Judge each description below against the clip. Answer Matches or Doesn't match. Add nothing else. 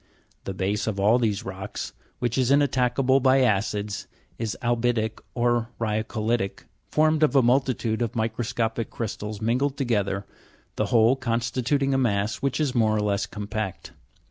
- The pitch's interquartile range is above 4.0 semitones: Doesn't match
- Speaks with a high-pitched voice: Doesn't match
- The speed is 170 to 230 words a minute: Doesn't match